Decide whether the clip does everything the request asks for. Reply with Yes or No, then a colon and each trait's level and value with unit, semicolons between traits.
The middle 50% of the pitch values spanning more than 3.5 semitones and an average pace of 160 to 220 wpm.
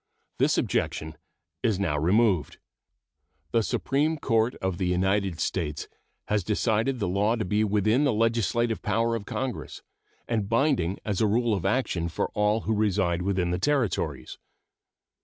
No: average, 3.9 semitones; average, 150 wpm